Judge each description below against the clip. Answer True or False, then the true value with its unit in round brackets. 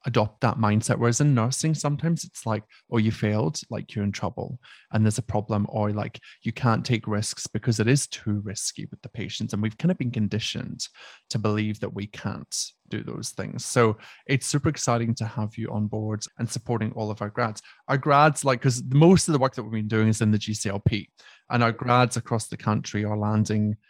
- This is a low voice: True (115 Hz)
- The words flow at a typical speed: False (220 wpm)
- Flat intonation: False (3.2 semitones)